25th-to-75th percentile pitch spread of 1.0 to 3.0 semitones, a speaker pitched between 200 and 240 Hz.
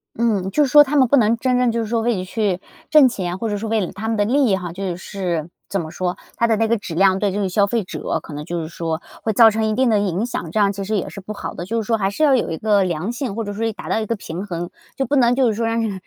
No: average, 3.6 semitones; high, 210 Hz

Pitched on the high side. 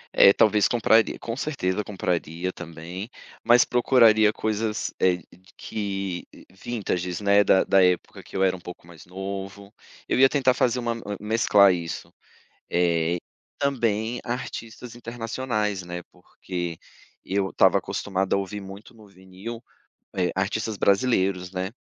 No: low, 100 Hz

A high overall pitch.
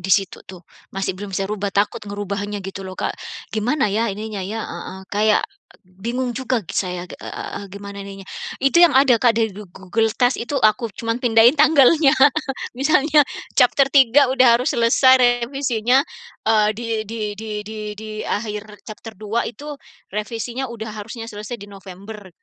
Yes: high, 220 Hz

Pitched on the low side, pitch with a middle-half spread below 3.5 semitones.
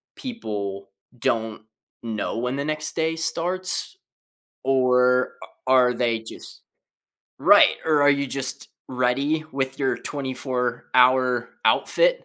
Yes: low, 130 Hz; average, 3.0 semitones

